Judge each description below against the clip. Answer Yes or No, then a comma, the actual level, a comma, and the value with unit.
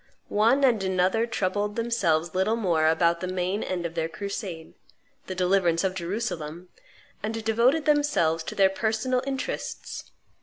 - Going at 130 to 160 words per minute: Yes, average, 145 wpm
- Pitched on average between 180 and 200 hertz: Yes, high, 190 Hz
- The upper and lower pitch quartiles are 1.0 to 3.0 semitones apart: No, average, 4.8 semitones